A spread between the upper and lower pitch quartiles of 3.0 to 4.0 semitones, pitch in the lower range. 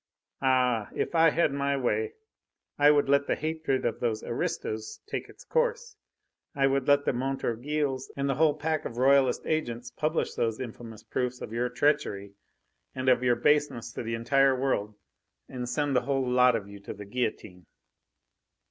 Yes: average, 3.5 semitones; low, 130 Hz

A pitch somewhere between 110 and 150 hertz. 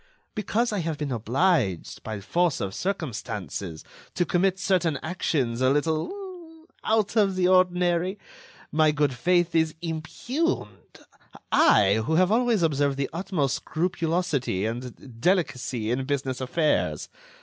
No: medium, 160 Hz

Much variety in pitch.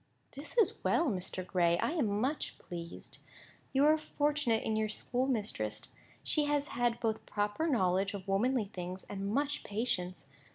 Yes: wide, 6.6 semitones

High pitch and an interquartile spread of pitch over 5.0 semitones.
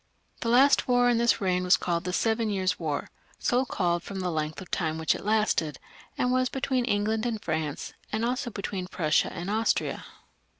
Yes: high, 205 Hz; wide, 5.5 semitones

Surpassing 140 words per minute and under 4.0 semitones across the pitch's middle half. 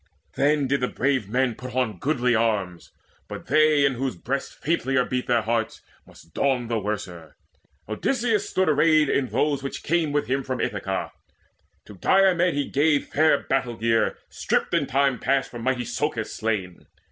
No: average, 170 wpm; average, 4.3 semitones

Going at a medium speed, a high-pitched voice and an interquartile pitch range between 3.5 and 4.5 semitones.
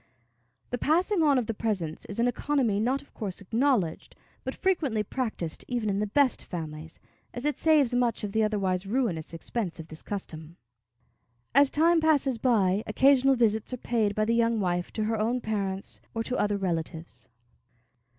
No: average, 175 wpm; high, 220 Hz; average, 4.9 semitones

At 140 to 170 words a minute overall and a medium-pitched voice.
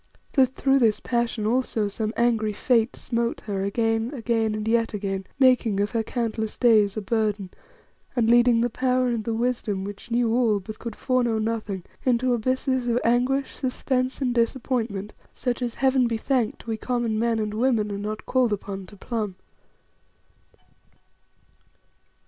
No: average, 160 wpm; high, 230 Hz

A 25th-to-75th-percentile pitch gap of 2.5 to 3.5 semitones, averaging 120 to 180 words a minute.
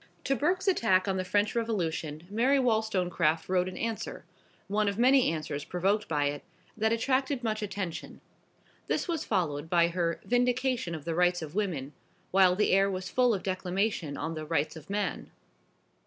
No: average, 5.2 semitones; average, 170 wpm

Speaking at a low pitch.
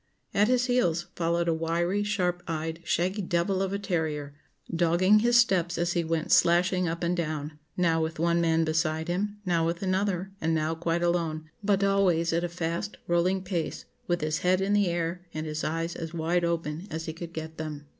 No: medium, 170 Hz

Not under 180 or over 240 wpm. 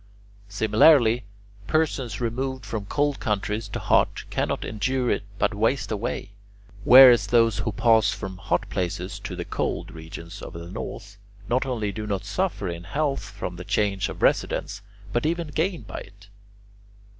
No: average, 155 wpm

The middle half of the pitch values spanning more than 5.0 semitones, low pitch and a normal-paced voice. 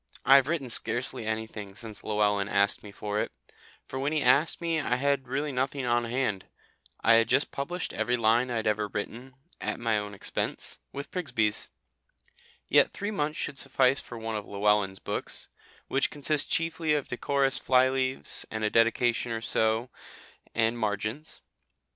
No: average, 4.2 semitones; low, 120 Hz; average, 170 wpm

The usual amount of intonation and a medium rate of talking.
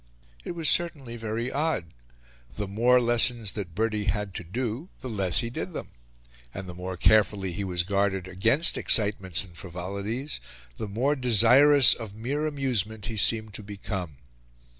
Yes: average, 4.2 semitones; average, 160 wpm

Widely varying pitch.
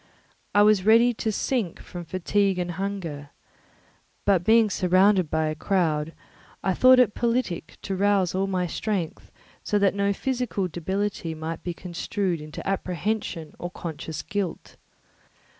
No: average, 3.3 semitones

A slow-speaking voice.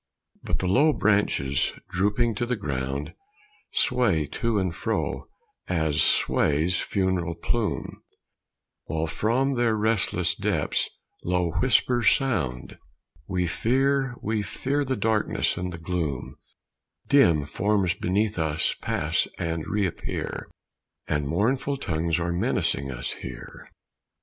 Yes: slow, 115 wpm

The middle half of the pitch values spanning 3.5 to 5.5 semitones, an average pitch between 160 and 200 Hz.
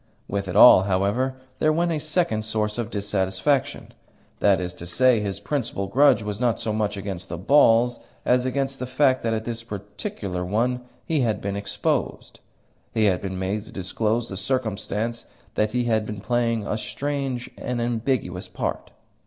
No: average, 3.9 semitones; low, 110 Hz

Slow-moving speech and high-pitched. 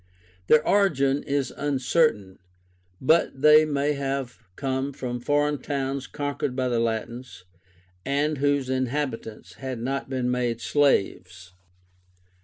No: slow, 115 wpm; low, 135 Hz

